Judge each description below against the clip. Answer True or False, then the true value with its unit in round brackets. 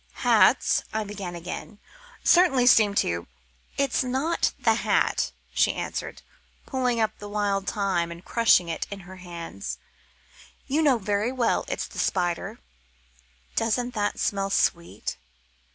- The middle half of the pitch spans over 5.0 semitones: True (5.5 semitones)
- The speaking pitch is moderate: False (205 Hz)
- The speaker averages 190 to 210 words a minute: False (135 wpm)